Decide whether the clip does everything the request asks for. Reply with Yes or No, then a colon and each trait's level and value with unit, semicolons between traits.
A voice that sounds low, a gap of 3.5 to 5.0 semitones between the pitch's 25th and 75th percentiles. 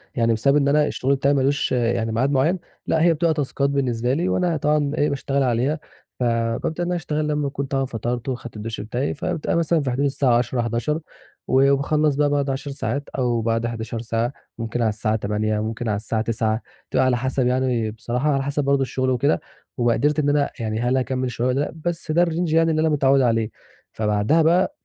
Yes: low, 130 Hz; average, 3.9 semitones